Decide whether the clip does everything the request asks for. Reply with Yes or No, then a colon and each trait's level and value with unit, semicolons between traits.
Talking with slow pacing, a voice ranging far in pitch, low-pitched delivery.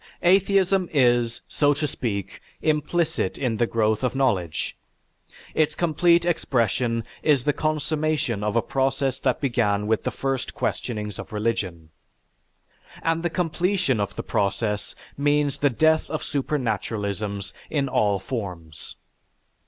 Yes: slow, 130 wpm; wide, 6.5 semitones; low, 130 Hz